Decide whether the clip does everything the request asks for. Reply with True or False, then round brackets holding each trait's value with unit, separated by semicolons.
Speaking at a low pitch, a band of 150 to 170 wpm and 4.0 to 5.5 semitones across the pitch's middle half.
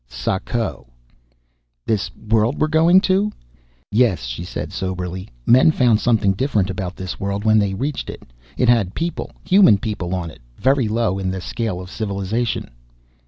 True (105 Hz; 160 wpm; 4.6 semitones)